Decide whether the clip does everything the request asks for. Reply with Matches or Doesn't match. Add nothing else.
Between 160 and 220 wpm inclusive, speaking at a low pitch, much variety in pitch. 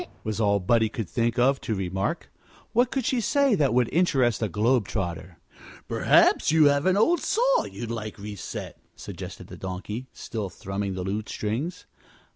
Matches